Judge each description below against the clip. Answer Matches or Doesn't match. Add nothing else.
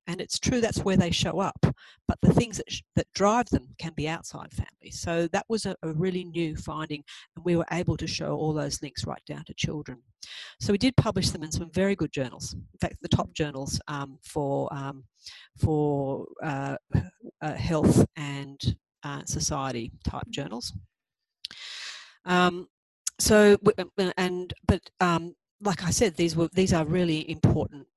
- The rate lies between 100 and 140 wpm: Doesn't match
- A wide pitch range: Doesn't match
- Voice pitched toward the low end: Doesn't match